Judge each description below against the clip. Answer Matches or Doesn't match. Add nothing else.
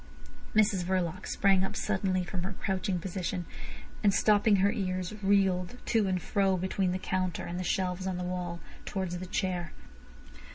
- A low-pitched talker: Doesn't match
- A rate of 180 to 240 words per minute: Doesn't match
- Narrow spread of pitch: Matches